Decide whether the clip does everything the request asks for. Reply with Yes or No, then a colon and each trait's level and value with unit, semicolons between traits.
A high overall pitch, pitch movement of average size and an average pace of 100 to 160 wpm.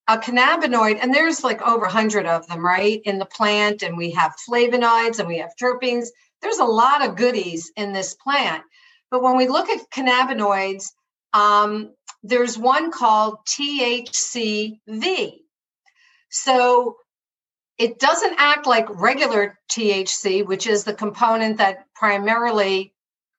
Yes: high, 230 Hz; average, 3.7 semitones; average, 140 wpm